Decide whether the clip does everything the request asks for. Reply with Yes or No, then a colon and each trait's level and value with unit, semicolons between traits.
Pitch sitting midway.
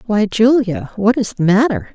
No: high, 215 Hz